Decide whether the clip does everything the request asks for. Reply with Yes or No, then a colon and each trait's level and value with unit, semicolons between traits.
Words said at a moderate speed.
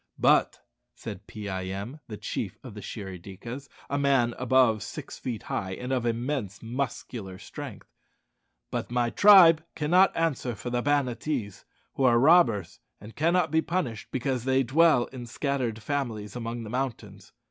Yes: average, 160 wpm